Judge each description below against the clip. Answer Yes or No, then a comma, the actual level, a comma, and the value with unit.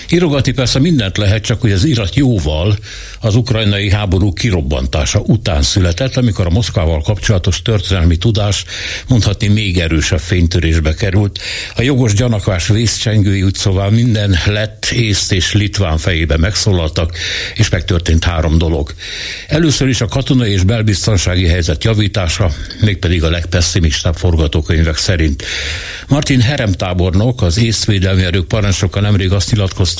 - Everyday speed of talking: Yes, average, 130 wpm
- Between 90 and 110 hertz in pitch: Yes, low, 100 Hz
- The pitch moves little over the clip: No, average, 3.9 semitones